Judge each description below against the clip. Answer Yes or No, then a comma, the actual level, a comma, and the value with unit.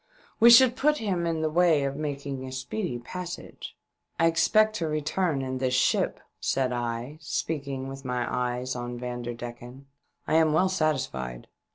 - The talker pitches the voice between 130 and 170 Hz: Yes, medium, 140 Hz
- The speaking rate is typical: Yes, average, 165 wpm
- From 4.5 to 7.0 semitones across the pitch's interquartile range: Yes, average, 4.9 semitones